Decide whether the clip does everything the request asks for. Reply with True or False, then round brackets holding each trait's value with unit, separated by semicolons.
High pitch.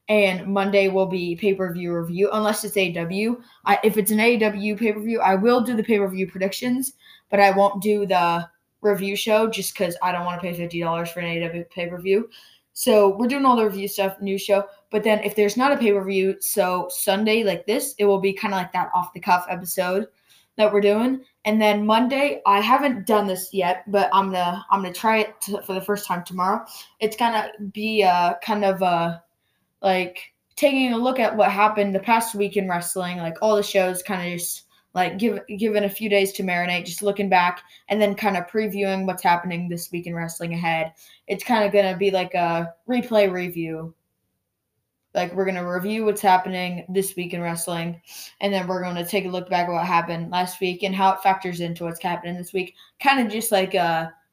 True (195 Hz)